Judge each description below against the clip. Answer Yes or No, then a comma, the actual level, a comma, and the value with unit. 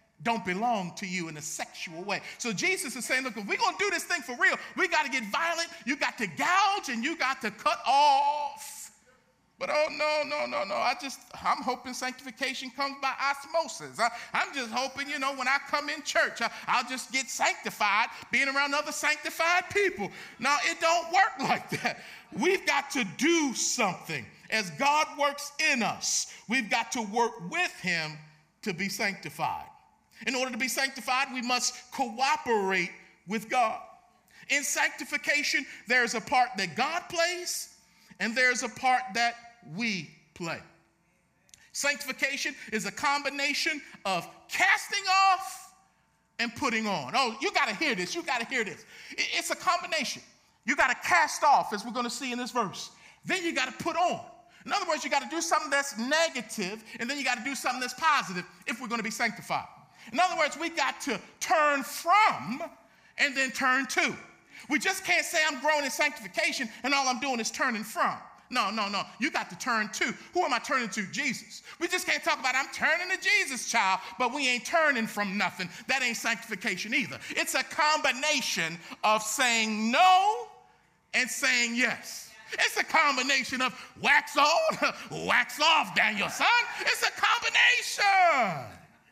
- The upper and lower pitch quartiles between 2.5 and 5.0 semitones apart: No, wide, 5.4 semitones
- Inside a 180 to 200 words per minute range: Yes, average, 185 wpm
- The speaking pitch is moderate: No, very high, 275 Hz